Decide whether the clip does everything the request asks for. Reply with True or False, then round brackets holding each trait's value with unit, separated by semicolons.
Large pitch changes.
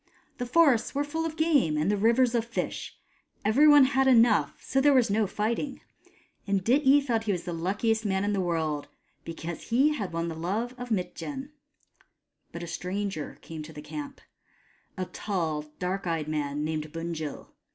True (7.6 semitones)